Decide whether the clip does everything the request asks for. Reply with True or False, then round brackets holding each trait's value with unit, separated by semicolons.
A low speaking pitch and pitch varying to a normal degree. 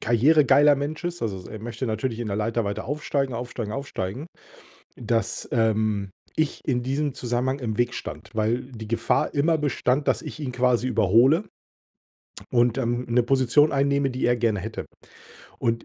True (120 Hz; 3.6 semitones)